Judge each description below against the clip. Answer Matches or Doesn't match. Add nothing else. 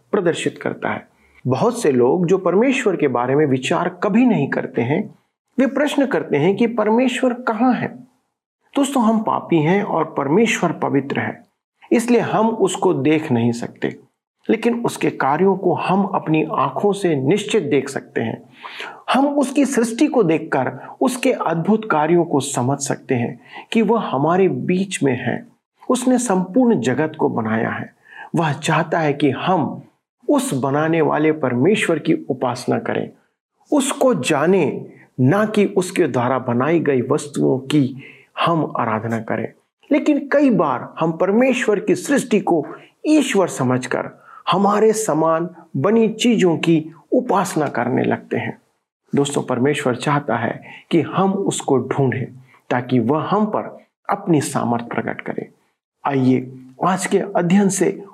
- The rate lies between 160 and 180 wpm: Doesn't match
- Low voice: Doesn't match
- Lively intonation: Matches